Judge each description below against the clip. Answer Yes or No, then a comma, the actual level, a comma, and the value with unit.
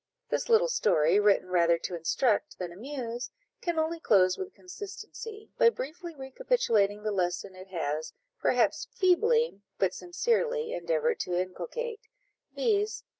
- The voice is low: No, very high, 295 Hz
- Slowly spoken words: Yes, slow, 130 wpm